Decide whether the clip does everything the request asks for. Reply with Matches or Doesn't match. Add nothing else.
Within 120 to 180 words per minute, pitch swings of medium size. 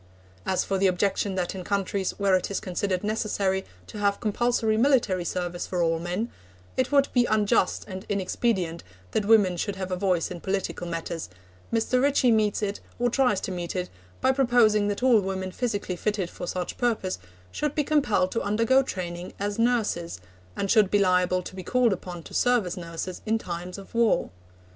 Doesn't match